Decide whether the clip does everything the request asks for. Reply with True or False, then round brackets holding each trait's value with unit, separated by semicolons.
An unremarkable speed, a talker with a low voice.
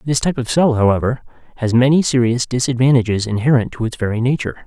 True (180 wpm; 125 Hz)